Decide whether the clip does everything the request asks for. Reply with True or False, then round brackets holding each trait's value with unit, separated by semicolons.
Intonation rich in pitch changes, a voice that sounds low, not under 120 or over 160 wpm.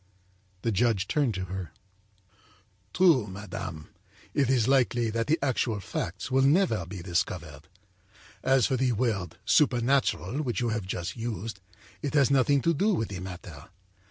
True (5.9 semitones; 115 Hz; 155 wpm)